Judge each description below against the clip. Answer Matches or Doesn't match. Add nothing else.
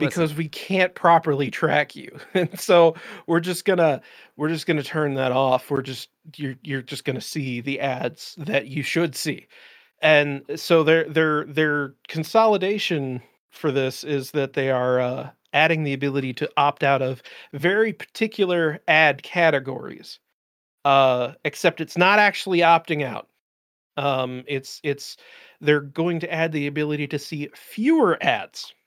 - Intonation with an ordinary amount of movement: Matches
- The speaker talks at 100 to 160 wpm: Matches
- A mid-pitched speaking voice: Matches